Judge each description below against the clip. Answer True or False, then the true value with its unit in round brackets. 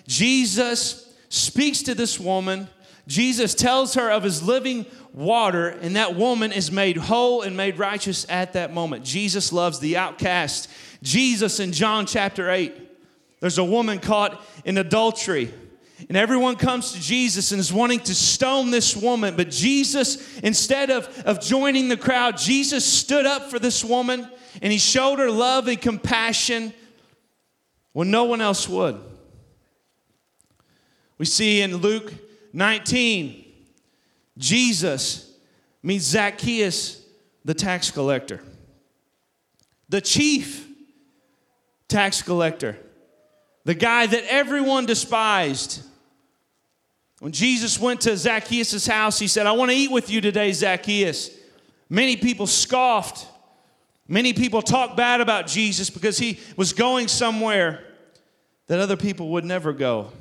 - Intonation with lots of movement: False (4.6 semitones)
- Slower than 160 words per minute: True (135 wpm)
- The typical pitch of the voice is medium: False (215 Hz)